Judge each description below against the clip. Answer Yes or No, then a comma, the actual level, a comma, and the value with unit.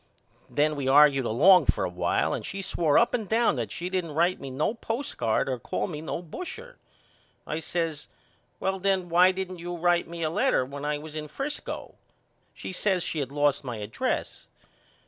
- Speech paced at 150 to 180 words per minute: No, average, 190 wpm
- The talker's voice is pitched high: No, medium, 165 Hz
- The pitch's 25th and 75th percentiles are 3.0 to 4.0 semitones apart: No, average, 4.5 semitones